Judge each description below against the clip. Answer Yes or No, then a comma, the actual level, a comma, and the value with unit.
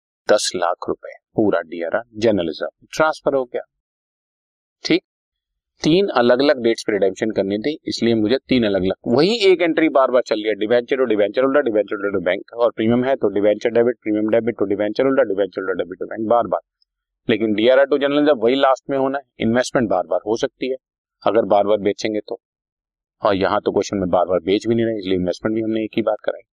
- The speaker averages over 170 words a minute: Yes, fast, 190 wpm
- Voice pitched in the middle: No, low, 115 Hz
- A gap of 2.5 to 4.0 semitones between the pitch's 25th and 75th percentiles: No, average, 4.4 semitones